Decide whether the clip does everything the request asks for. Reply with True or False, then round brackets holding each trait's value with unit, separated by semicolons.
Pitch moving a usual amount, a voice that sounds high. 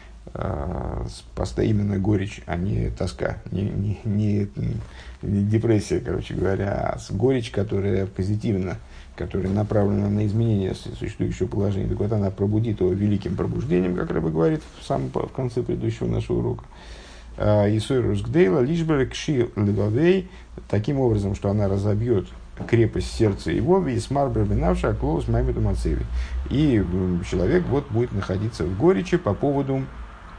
False (3.8 semitones; 105 Hz)